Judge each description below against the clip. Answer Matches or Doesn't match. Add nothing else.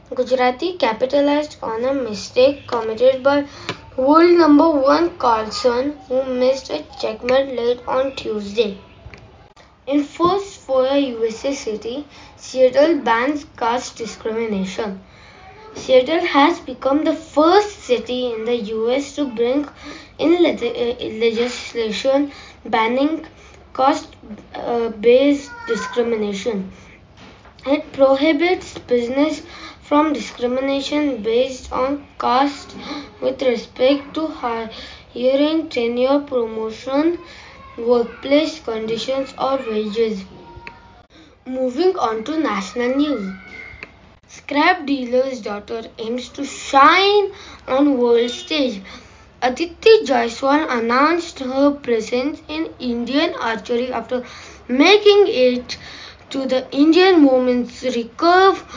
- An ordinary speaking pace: Doesn't match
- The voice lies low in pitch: Doesn't match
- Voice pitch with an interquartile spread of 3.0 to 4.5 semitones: Matches